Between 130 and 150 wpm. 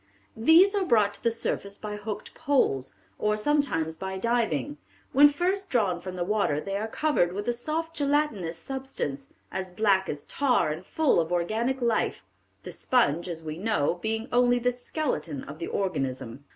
No: average, 175 wpm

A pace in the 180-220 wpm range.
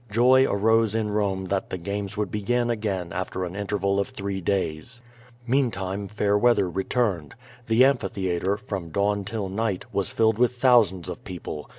No: average, 165 wpm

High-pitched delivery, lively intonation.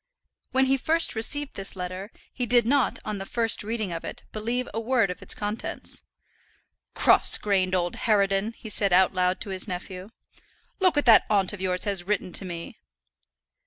No: high, 205 Hz; average, 3.9 semitones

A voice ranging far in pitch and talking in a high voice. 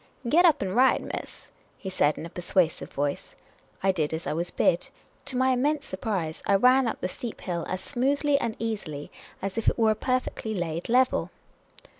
Yes: wide, 6.5 semitones; high, 215 Hz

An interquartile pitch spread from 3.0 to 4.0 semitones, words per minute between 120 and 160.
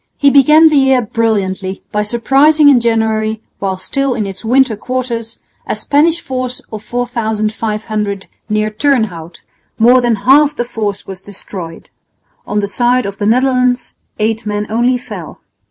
Yes: average, 3.4 semitones; average, 150 wpm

